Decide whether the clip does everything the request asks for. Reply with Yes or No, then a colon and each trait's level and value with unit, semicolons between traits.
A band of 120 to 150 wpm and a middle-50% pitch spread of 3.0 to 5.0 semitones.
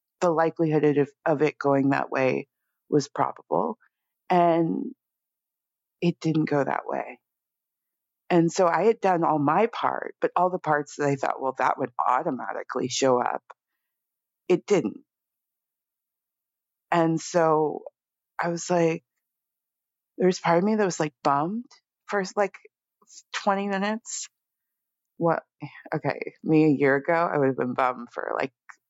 Yes: average, 145 wpm; average, 3.9 semitones